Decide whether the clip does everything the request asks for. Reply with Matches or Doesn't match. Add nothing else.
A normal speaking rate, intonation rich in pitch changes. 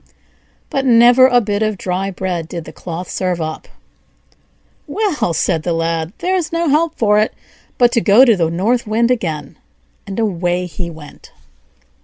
Matches